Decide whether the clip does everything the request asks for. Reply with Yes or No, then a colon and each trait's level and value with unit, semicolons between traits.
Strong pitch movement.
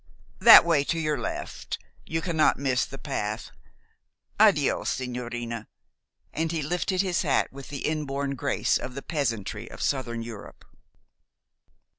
No: average, 4.7 semitones